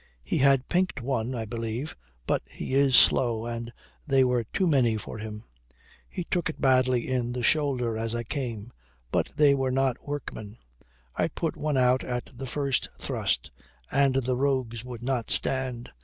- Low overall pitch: Yes, low, 125 Hz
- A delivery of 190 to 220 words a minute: No, average, 170 wpm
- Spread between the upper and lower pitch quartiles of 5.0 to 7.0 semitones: No, narrow, 2.6 semitones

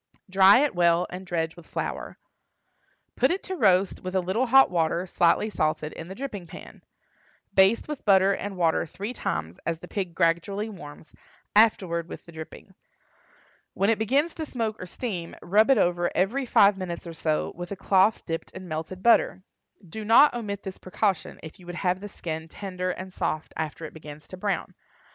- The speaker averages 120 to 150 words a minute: No, average, 190 wpm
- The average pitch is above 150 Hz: Yes, medium, 185 Hz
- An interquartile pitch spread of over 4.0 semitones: No, average, 3.7 semitones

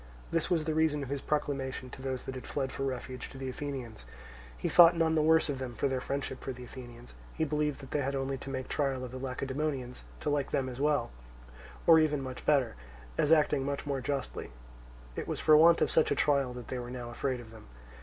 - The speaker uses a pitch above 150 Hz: No, low, 135 Hz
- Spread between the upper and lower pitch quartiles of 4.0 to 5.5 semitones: No, narrow, 2.6 semitones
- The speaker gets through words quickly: Yes, fast, 235 wpm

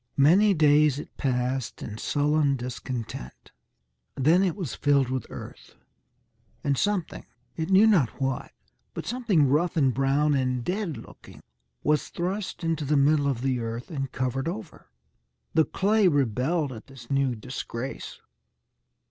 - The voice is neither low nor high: Yes, medium, 145 Hz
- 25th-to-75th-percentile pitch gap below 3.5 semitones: No, average, 4.3 semitones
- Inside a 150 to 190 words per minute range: No, average, 140 wpm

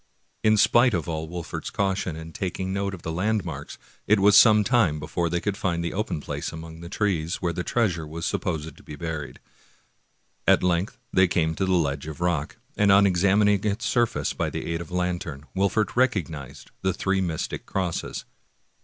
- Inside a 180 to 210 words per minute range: Yes, average, 195 wpm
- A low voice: Yes, very low, 90 Hz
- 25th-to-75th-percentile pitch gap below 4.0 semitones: Yes, average, 3.5 semitones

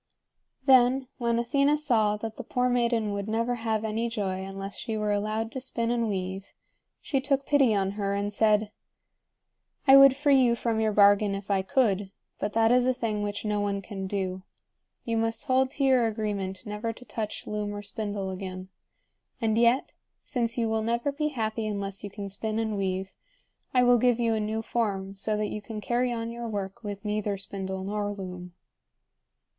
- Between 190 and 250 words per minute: Yes, average, 195 wpm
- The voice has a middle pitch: No, high, 215 Hz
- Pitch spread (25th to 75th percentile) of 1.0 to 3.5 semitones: Yes, average, 2.8 semitones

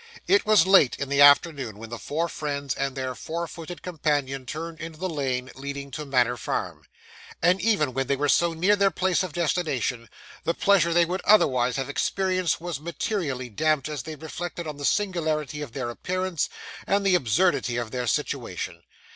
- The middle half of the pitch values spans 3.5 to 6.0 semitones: Yes, average, 4.7 semitones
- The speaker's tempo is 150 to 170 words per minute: No, average, 185 wpm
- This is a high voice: No, medium, 155 Hz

